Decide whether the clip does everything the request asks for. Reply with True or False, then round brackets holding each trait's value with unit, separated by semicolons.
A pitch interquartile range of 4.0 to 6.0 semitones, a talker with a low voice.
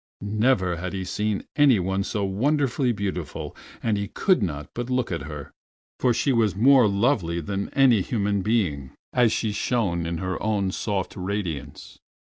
True (4.6 semitones; 100 Hz)